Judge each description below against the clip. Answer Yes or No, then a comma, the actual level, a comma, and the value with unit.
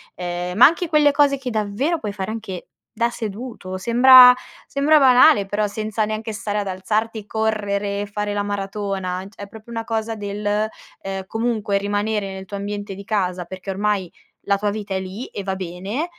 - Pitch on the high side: Yes, high, 205 Hz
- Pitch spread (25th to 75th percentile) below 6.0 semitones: Yes, narrow, 2.4 semitones